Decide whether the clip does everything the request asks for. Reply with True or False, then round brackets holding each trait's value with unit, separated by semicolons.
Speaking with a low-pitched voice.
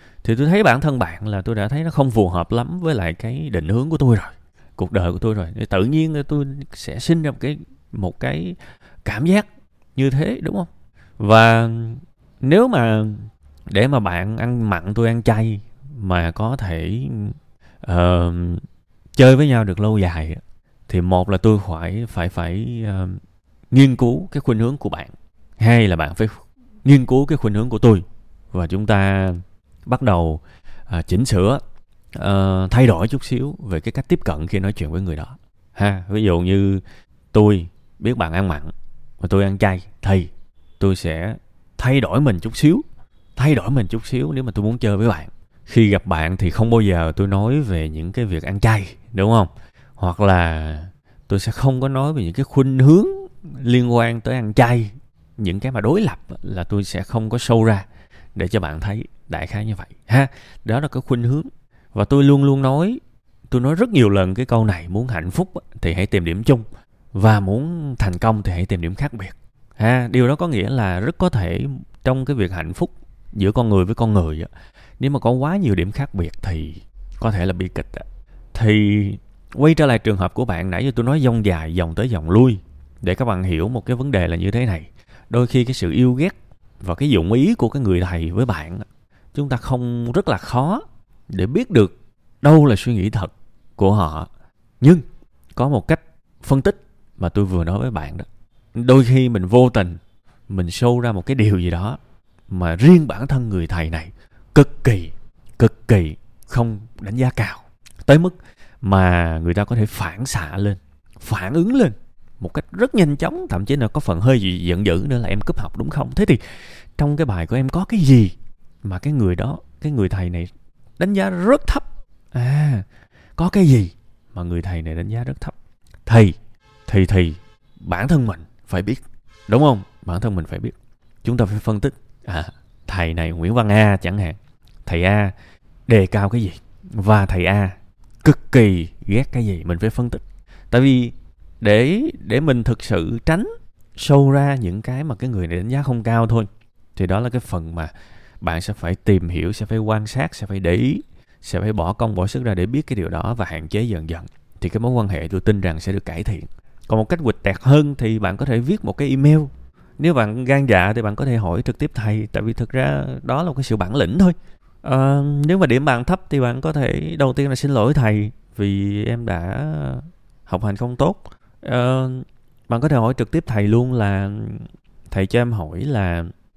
True (110 Hz)